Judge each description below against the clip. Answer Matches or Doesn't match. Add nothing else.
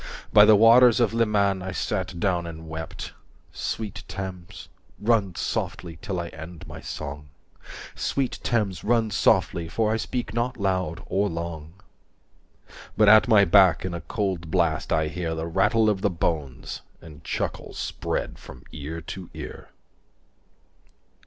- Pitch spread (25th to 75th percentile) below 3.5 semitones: Doesn't match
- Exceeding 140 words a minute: Matches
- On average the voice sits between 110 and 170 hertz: Doesn't match